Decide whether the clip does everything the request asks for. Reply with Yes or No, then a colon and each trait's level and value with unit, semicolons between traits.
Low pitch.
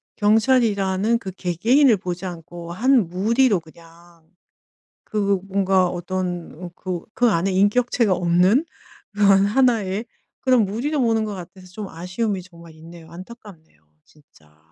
No: high, 190 Hz